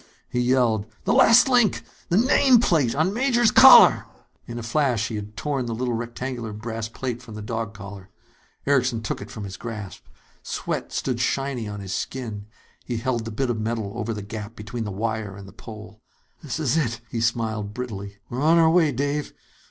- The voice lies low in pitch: Yes, low, 115 Hz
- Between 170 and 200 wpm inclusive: Yes, average, 185 wpm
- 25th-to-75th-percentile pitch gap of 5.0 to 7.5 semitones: No, average, 3.8 semitones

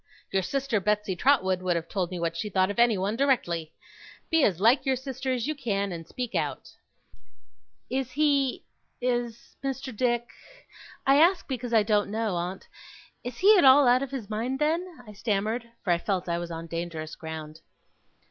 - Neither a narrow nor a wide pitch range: No, wide, 6.1 semitones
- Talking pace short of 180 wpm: No, average, 185 wpm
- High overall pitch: Yes, high, 225 Hz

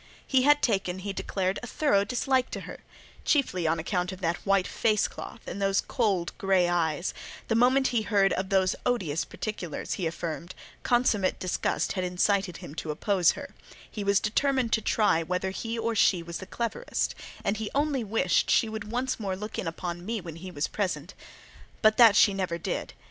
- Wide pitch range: No, average, 4.0 semitones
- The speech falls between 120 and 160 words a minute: No, average, 190 wpm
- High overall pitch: Yes, high, 195 Hz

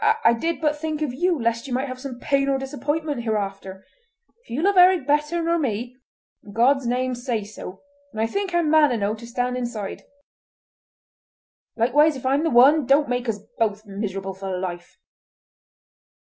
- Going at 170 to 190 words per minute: Yes, average, 175 wpm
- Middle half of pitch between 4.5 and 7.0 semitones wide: Yes, average, 5.1 semitones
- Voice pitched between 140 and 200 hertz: No, very high, 255 Hz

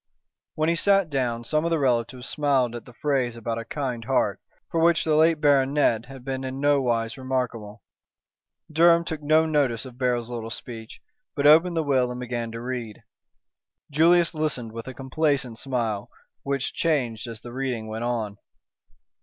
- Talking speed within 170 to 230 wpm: Yes, average, 175 wpm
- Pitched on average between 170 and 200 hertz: No, low, 130 Hz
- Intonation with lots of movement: No, average, 4.3 semitones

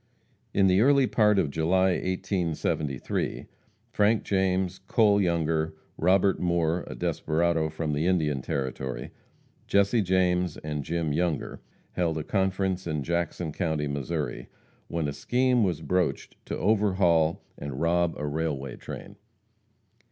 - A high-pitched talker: No, very low, 85 Hz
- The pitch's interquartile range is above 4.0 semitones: No, average, 3.4 semitones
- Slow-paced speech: Yes, slow, 130 wpm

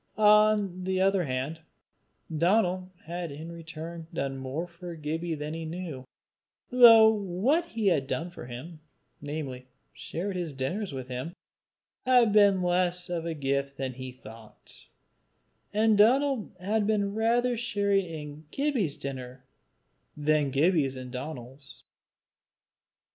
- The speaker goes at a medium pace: No, slow, 130 wpm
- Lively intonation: Yes, wide, 6.4 semitones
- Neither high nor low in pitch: Yes, medium, 170 Hz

